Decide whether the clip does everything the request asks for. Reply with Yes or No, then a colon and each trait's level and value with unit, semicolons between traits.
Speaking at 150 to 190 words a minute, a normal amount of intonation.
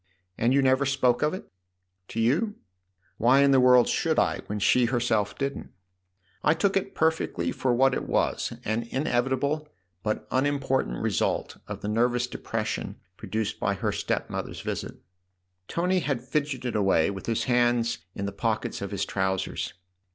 Yes: average, 165 wpm; average, 4.4 semitones